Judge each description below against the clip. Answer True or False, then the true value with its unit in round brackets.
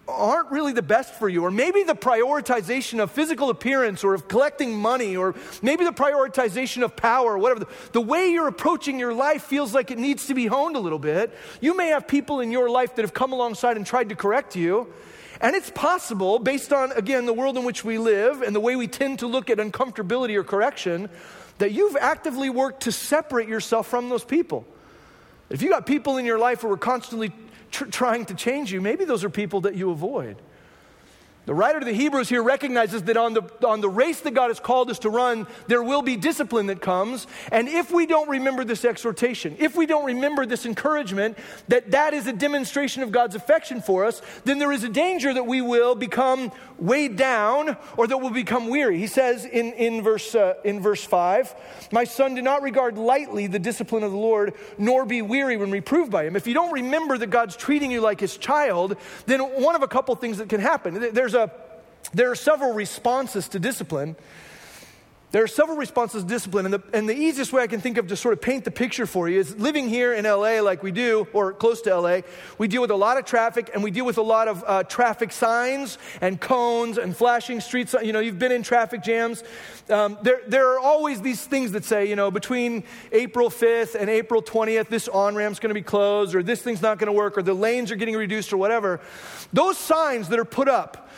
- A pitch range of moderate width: True (3.6 semitones)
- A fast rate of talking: True (225 wpm)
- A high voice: True (240 Hz)